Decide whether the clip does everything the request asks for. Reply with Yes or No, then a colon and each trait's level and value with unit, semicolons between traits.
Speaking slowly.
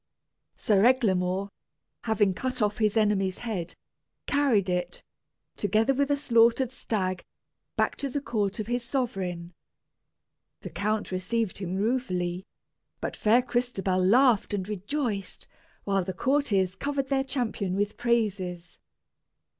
Yes: slow, 125 wpm